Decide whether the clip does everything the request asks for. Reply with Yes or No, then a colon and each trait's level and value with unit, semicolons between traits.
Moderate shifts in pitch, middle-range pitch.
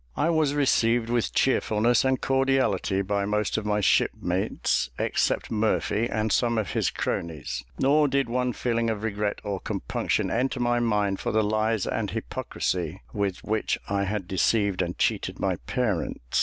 No: average, 3.3 semitones; low, 110 Hz